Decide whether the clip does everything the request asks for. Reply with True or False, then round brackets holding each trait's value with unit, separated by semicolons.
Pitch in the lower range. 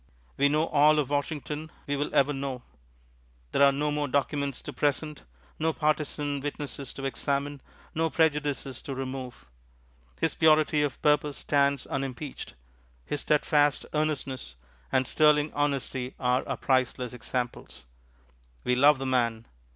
False (145 Hz)